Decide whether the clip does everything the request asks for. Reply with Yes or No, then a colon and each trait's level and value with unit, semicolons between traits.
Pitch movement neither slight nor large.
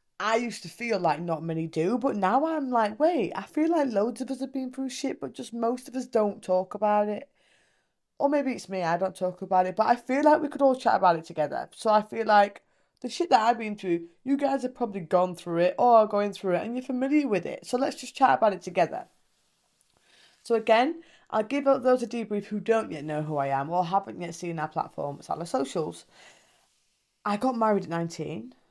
No: wide, 6.0 semitones